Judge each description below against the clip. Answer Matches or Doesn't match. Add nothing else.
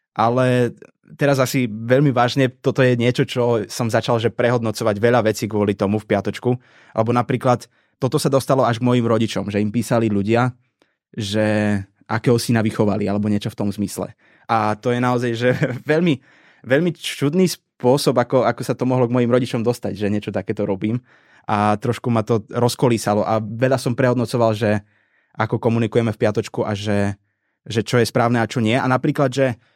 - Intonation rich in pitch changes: Doesn't match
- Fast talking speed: Matches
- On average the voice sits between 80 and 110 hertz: Doesn't match